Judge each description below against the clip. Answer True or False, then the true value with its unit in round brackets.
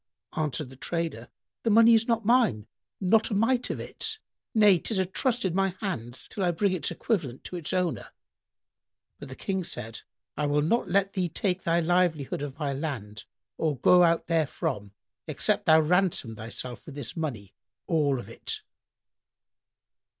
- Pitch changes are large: True (5.8 semitones)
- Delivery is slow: False (170 wpm)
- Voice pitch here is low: False (170 Hz)